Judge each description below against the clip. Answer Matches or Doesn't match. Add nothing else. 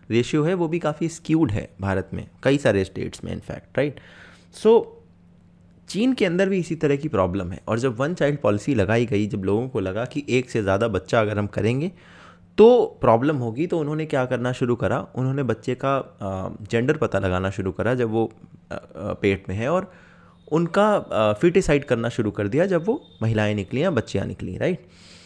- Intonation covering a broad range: Matches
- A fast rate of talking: Matches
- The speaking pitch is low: Matches